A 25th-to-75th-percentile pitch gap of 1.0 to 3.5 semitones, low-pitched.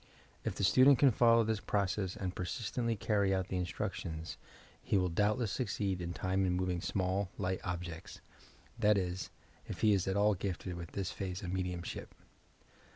Yes: narrow, 2.5 semitones; very low, 95 Hz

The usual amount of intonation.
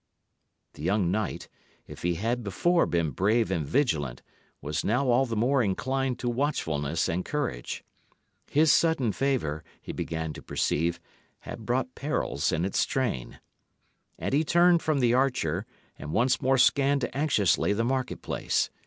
No: wide, 8.0 semitones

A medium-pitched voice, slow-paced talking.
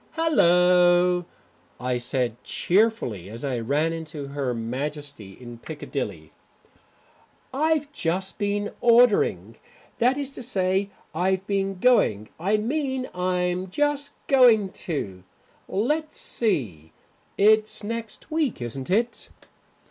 Yes: medium, 180 Hz; slow, 110 wpm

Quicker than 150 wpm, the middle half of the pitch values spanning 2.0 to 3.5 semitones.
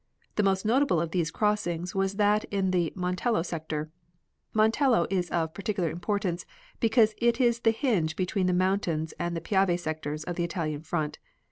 No: average, 170 wpm; average, 4.0 semitones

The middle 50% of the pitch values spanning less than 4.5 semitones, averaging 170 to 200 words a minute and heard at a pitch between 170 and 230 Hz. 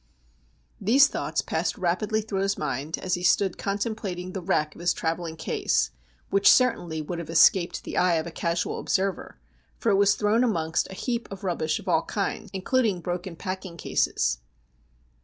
Yes: average, 3.2 semitones; average, 175 wpm; medium, 185 Hz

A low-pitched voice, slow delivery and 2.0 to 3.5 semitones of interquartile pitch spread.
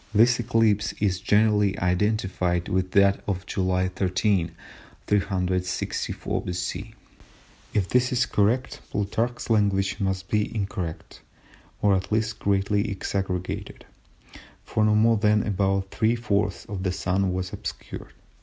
Yes: low, 100 Hz; slow, 125 wpm; narrow, 2.4 semitones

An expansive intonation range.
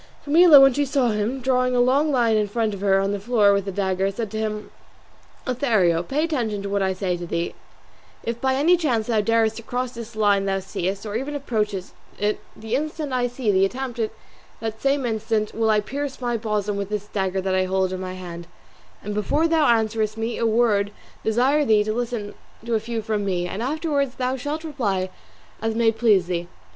No: average, 3.9 semitones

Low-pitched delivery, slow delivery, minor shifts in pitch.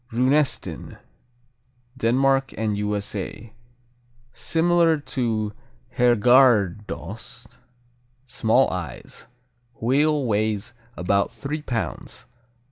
No: low, 120 Hz; slow, 65 wpm; average, 4.4 semitones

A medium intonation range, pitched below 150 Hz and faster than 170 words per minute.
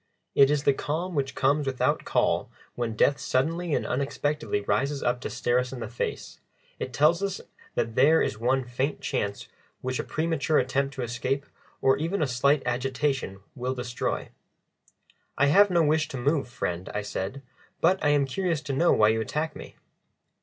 Yes: average, 3.6 semitones; low, 135 Hz; average, 180 wpm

